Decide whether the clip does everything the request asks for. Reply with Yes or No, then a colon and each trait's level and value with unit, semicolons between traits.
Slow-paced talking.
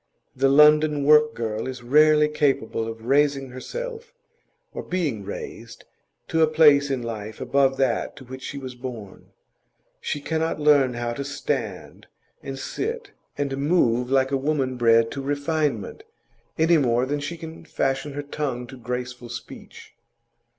No: average, 150 wpm